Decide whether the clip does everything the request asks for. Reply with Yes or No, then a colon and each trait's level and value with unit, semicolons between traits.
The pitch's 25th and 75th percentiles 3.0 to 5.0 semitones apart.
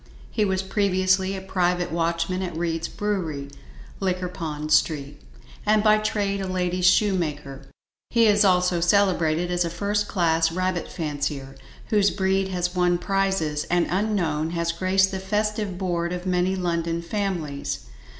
No: narrow, 2.6 semitones